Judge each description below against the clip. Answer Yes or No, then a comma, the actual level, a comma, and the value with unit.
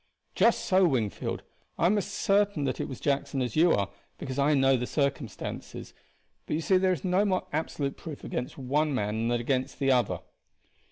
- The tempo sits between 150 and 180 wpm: No, average, 190 wpm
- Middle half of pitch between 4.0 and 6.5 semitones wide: Yes, average, 5.0 semitones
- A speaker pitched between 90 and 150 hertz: Yes, medium, 140 Hz